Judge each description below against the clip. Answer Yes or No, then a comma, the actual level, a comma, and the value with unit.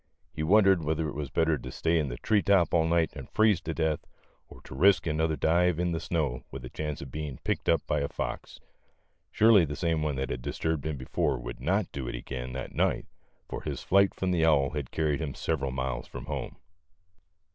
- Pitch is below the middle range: Yes, very low, 80 Hz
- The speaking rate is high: Yes, fast, 220 wpm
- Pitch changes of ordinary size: Yes, average, 3.9 semitones